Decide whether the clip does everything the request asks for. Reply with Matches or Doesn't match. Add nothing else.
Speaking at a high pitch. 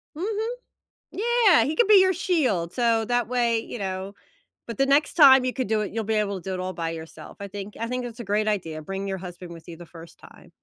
Matches